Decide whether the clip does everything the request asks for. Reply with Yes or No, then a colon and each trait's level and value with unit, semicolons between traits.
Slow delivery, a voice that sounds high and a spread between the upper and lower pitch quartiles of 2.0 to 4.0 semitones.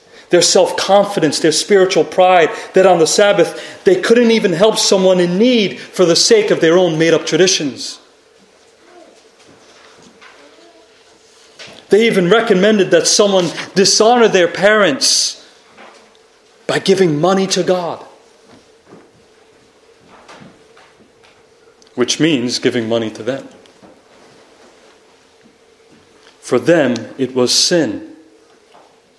No: slow, 105 wpm; high, 195 Hz; wide, 5.5 semitones